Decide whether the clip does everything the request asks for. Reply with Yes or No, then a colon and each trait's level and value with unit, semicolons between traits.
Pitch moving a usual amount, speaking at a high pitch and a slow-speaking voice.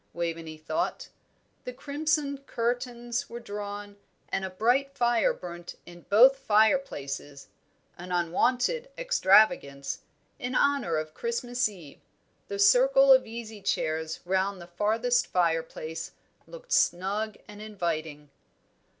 No: wide, 6.4 semitones; high, 210 Hz; slow, 115 wpm